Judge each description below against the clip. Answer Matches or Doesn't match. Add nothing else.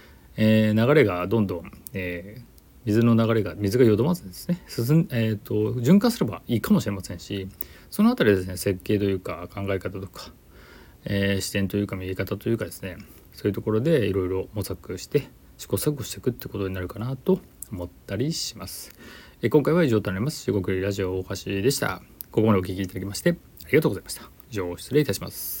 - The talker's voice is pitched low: Matches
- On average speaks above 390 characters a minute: Matches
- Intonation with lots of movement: Doesn't match